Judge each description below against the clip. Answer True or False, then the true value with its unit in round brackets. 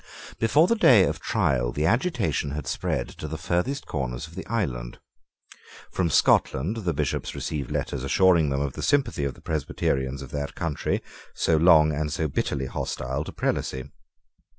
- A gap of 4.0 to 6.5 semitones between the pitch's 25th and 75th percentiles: True (4.8 semitones)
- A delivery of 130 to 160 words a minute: False (170 wpm)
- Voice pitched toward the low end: True (75 Hz)